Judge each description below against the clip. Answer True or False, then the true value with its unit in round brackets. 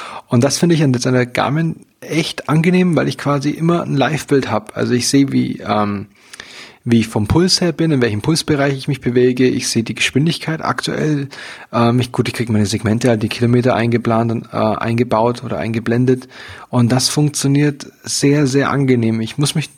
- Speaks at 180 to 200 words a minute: True (190 wpm)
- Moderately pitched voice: False (130 Hz)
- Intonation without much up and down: False (3.7 semitones)